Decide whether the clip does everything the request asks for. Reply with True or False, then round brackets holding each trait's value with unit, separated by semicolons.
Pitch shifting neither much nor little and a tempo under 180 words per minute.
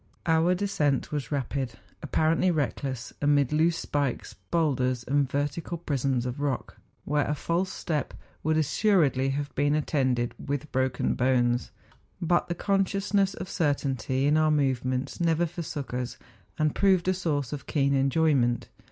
True (3.7 semitones; 150 wpm)